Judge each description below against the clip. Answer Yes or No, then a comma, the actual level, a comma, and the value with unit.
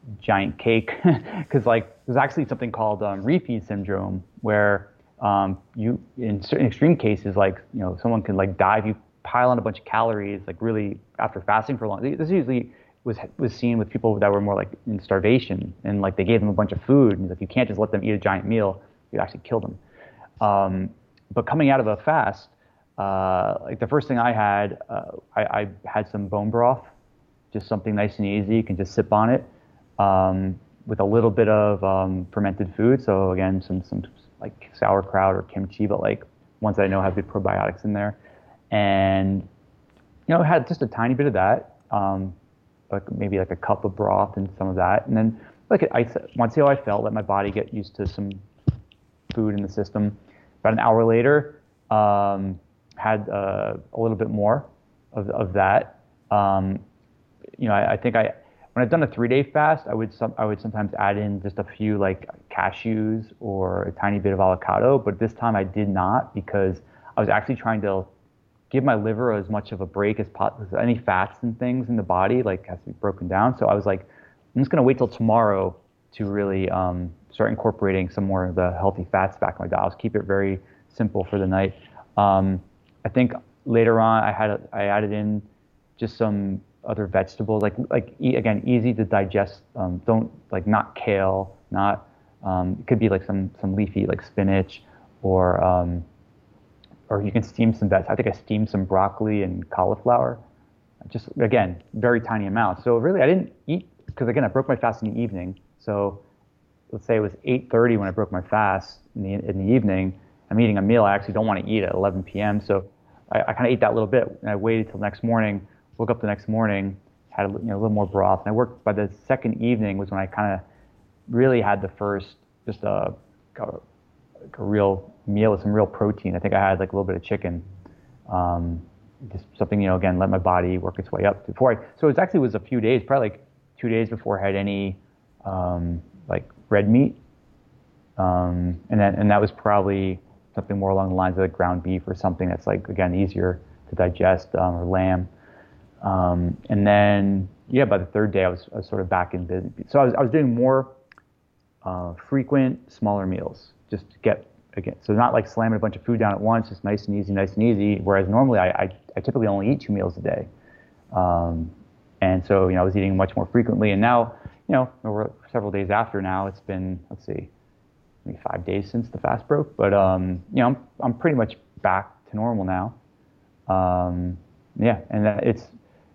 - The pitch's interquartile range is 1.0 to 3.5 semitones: Yes, average, 2.8 semitones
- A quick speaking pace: Yes, fast, 215 wpm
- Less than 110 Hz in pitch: Yes, low, 100 Hz